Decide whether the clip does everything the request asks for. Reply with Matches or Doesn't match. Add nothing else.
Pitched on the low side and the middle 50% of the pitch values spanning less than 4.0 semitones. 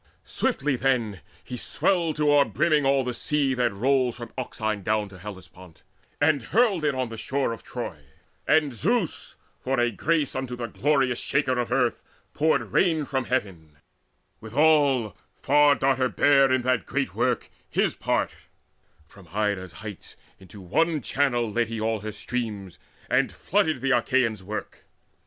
Doesn't match